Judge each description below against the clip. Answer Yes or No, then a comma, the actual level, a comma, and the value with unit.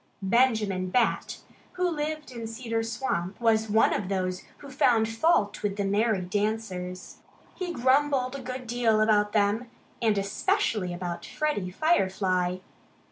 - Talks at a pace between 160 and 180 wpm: No, slow, 135 wpm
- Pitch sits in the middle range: No, high, 220 Hz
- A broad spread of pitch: No, average, 4.5 semitones